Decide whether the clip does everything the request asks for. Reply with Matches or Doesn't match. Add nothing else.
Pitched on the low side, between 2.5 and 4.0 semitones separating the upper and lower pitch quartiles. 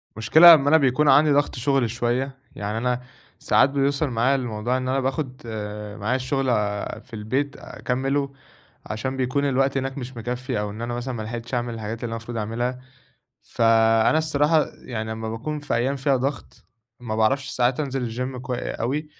Matches